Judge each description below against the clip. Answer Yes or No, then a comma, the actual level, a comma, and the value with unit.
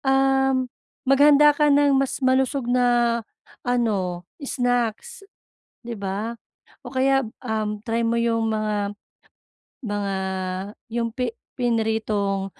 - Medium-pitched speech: No, high, 235 Hz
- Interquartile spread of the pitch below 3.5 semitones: No, average, 3.8 semitones